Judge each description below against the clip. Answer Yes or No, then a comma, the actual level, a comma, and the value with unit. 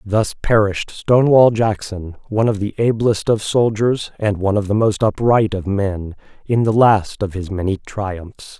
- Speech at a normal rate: Yes, average, 175 wpm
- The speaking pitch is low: Yes, low, 105 Hz